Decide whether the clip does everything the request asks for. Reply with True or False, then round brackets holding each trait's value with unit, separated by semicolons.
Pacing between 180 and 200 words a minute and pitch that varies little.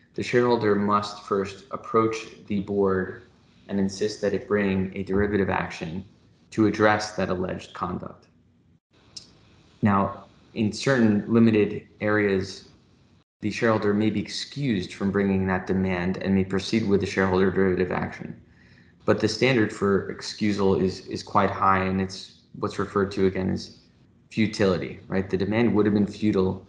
False (150 wpm; 1.9 semitones)